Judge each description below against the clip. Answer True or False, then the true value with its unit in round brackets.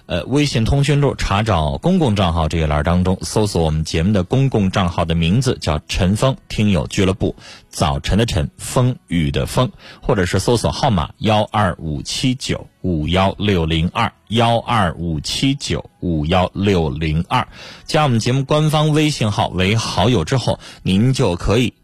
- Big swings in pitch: True (6.0 semitones)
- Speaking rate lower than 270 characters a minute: True (255 characters per minute)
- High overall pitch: False (100 Hz)